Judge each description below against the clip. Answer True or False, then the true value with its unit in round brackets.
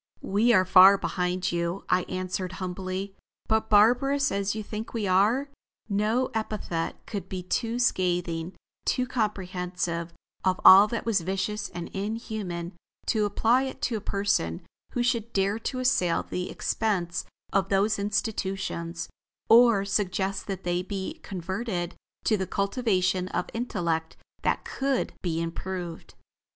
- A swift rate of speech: False (135 wpm)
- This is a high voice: True (195 Hz)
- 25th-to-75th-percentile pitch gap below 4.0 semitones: True (3.4 semitones)